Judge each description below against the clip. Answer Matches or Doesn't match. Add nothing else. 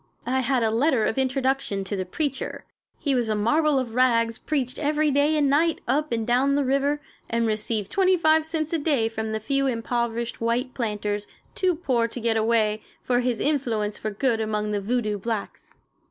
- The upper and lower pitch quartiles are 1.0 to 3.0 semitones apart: Doesn't match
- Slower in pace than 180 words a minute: Doesn't match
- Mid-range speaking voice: Doesn't match